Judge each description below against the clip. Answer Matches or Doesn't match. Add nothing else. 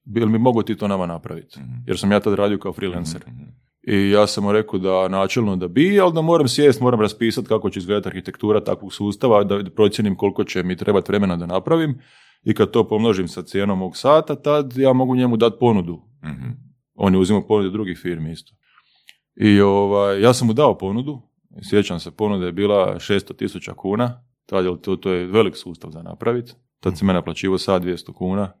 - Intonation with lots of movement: Doesn't match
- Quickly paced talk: Matches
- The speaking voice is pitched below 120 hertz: Matches